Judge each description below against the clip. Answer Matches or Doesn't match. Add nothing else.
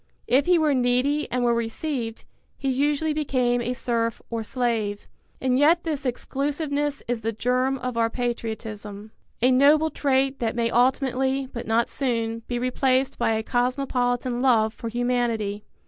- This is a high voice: Matches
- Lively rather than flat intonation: Doesn't match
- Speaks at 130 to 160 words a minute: Matches